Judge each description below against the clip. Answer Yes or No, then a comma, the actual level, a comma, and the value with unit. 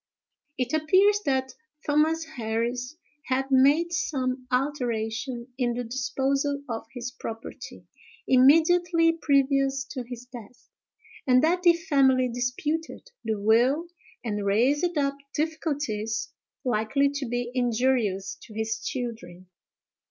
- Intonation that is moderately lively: Yes, average, 3.7 semitones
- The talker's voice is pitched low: No, very high, 260 Hz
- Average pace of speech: No, slow, 115 wpm